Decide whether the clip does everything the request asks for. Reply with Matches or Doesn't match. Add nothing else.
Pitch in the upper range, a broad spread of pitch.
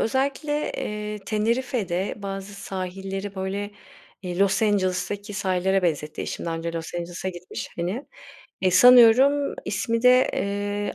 Doesn't match